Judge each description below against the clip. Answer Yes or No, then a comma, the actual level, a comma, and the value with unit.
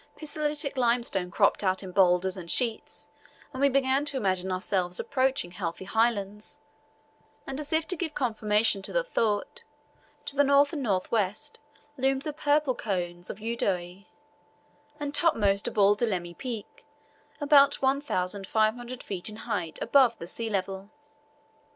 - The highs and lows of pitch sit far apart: Yes, wide, 6.4 semitones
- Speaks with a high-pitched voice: Yes, high, 225 Hz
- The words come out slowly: No, average, 145 wpm